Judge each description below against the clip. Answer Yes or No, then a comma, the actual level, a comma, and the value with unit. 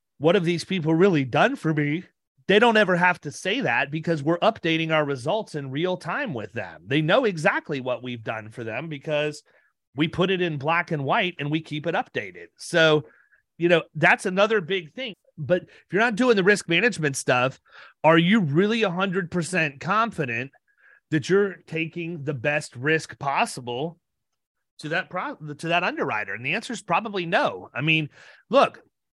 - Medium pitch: Yes, medium, 165 Hz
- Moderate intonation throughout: Yes, average, 4.2 semitones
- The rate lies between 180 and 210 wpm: Yes, average, 185 wpm